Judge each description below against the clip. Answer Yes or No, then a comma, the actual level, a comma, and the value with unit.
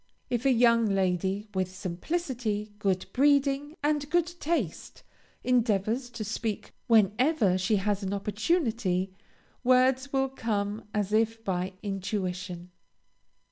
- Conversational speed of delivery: No, slow, 115 wpm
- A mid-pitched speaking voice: No, high, 215 Hz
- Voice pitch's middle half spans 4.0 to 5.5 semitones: Yes, average, 5.0 semitones